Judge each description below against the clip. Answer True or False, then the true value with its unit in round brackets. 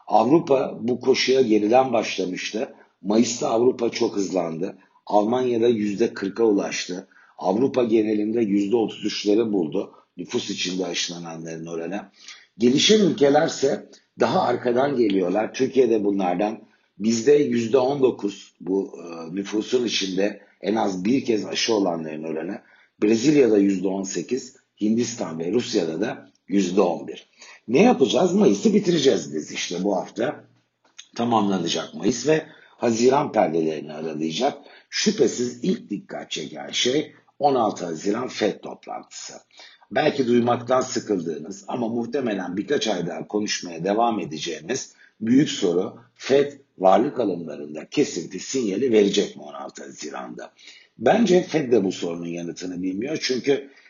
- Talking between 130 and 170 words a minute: False (110 wpm)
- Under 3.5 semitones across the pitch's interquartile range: False (5.1 semitones)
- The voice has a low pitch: True (110 Hz)